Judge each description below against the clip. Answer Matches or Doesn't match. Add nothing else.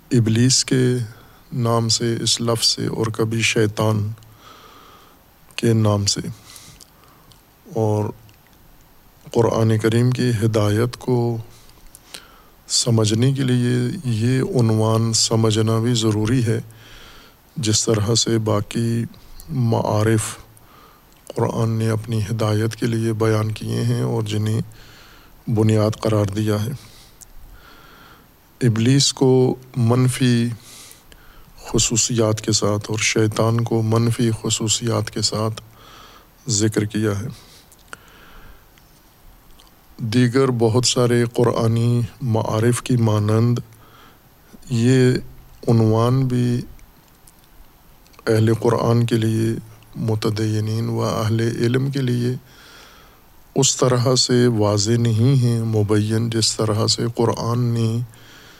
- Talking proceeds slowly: Matches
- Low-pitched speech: Matches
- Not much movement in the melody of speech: Matches